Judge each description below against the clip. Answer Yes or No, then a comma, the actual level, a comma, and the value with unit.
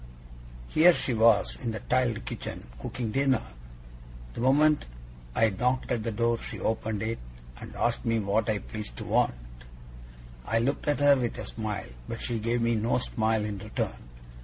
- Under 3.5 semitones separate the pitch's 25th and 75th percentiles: Yes, narrow, 2.5 semitones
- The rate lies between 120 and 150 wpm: No, average, 175 wpm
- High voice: No, low, 115 Hz